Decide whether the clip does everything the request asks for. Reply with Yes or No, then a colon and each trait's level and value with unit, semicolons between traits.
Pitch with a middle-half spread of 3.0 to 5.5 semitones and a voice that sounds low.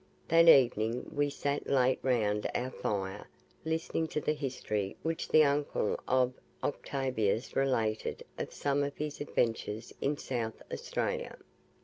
Yes: average, 4.4 semitones; low, 130 Hz